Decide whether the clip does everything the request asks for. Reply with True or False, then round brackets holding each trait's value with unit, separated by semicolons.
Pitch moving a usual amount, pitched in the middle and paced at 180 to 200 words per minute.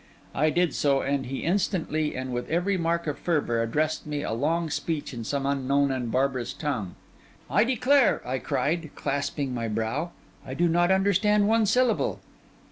False (4.7 semitones; 150 Hz; 170 wpm)